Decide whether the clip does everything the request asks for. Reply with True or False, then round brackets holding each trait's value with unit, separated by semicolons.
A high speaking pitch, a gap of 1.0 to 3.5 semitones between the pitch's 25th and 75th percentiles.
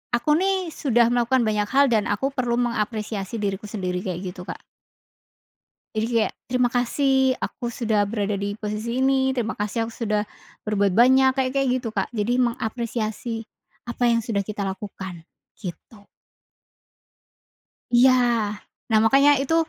True (225 Hz; 3.2 semitones)